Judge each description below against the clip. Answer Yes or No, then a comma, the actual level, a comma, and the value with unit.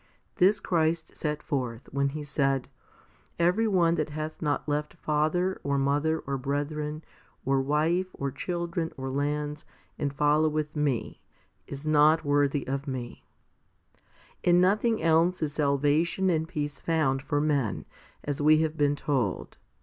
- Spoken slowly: No, average, 150 wpm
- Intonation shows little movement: Yes, narrow, 2.3 semitones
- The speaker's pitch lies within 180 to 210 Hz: No, medium, 150 Hz